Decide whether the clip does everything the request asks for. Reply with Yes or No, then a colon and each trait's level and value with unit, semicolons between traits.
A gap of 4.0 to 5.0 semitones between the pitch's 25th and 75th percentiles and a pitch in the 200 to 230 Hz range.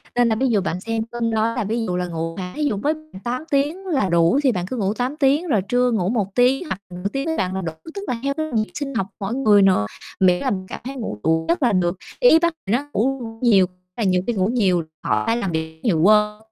No: wide, 5.6 semitones; high, 220 Hz